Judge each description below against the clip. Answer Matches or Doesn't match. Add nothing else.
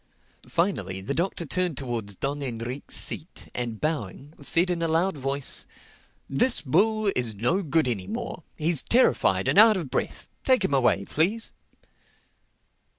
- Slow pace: Doesn't match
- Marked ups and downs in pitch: Matches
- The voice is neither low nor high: Matches